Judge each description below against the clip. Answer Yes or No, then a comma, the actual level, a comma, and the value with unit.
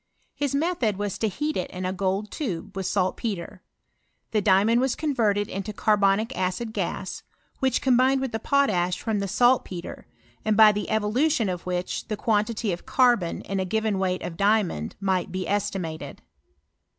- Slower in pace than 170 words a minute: Yes, average, 160 wpm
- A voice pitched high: Yes, high, 205 Hz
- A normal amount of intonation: Yes, average, 3.9 semitones